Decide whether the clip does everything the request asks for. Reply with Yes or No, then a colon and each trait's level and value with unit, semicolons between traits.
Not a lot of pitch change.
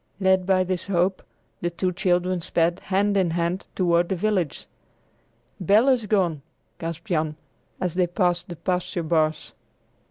Yes: narrow, 1.8 semitones